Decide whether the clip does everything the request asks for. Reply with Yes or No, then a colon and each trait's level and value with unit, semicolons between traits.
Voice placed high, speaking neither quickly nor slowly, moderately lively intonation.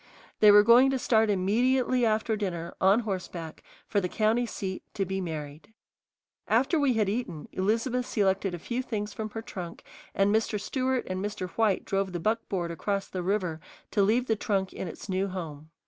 Yes: high, 205 Hz; average, 185 wpm; average, 3.3 semitones